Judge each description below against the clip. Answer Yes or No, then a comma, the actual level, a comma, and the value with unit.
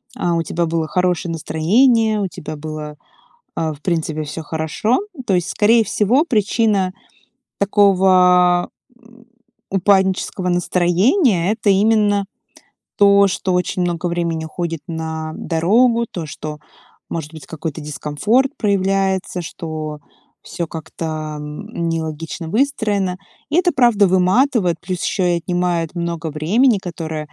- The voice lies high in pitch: No, medium, 180 Hz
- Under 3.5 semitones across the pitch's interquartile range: No, average, 4.0 semitones